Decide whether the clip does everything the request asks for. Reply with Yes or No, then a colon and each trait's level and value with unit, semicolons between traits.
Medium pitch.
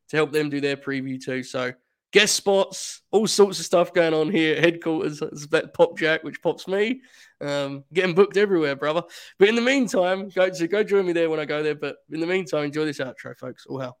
Yes: medium, 165 Hz